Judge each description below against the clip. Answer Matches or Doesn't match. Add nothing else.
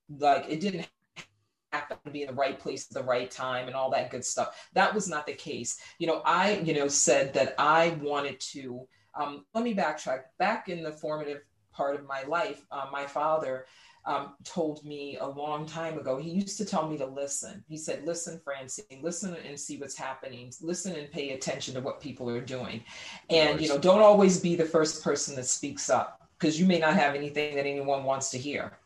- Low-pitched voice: Doesn't match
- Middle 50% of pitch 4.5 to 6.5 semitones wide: Doesn't match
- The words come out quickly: Matches